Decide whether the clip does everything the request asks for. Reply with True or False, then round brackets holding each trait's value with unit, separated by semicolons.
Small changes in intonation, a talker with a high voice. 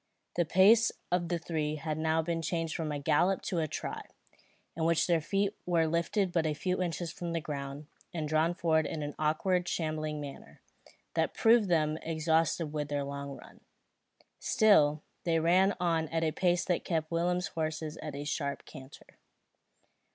False (2.3 semitones; 160 Hz)